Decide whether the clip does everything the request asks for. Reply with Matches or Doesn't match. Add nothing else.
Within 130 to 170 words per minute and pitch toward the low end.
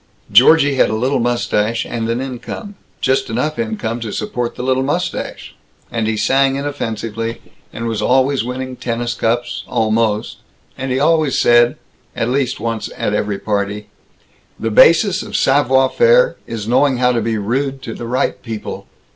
Matches